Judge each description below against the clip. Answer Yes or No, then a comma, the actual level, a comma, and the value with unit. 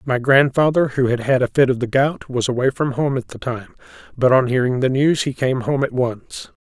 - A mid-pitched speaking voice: No, low, 130 Hz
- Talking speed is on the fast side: Yes, fast, 245 wpm